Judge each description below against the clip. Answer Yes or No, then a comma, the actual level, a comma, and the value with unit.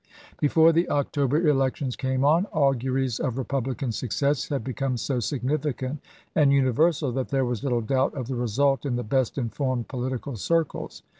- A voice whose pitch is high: No, low, 135 Hz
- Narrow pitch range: Yes, narrow, 2.3 semitones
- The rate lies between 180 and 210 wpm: No, average, 160 wpm